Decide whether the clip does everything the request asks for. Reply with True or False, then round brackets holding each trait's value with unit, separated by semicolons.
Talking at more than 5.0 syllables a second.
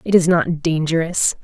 False (4.7 syllables/s)